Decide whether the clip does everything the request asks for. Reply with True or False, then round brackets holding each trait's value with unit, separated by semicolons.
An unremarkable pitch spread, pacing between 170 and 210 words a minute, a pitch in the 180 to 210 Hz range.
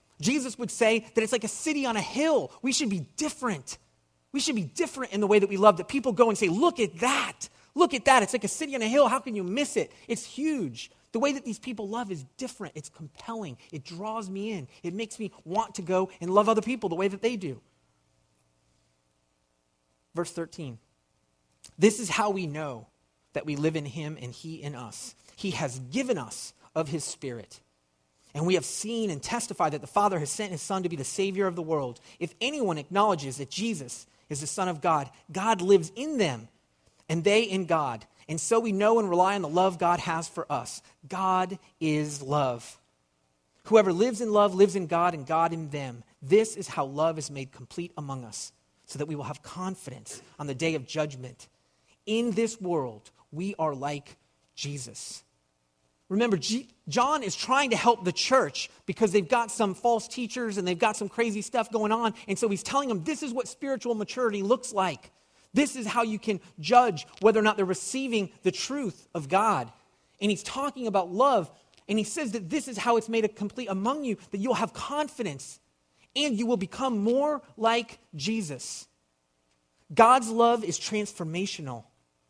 False (7.7 semitones; 200 wpm; 190 Hz)